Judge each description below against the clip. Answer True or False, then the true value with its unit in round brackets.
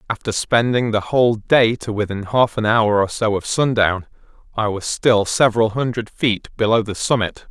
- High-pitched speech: False (110 Hz)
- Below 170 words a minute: False (185 wpm)